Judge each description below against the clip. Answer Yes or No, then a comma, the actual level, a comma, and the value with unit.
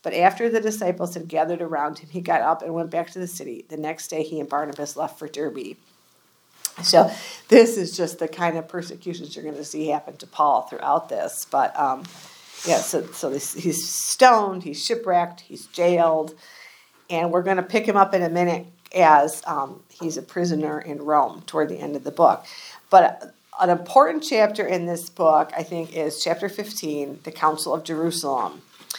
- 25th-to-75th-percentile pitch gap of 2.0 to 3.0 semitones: Yes, average, 2.7 semitones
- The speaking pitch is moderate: Yes, medium, 170 Hz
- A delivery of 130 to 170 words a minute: No, average, 195 wpm